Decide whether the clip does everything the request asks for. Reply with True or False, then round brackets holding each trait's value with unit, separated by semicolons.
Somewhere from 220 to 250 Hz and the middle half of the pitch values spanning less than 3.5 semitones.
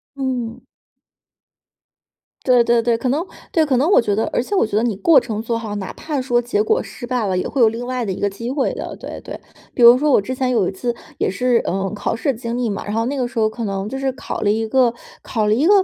True (235 Hz; 3.0 semitones)